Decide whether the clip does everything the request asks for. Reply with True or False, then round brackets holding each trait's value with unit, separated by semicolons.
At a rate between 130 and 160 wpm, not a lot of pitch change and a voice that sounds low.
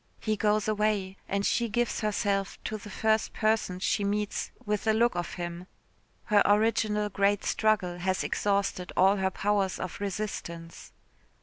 False (150 wpm; 2.0 semitones; 205 Hz)